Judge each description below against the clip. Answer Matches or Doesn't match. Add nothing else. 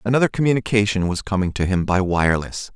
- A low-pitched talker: Matches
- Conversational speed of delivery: Matches